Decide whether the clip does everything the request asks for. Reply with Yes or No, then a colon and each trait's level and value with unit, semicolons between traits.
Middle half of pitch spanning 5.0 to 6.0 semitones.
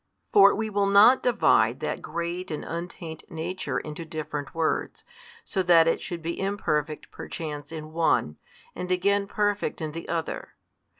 No: average, 3.8 semitones